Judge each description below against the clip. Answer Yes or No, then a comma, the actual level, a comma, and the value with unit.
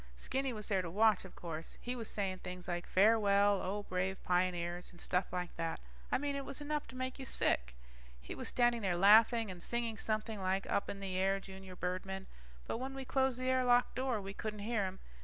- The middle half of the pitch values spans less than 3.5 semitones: No, average, 4.5 semitones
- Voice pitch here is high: Yes, high, 200 Hz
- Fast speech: Yes, fast, 220 wpm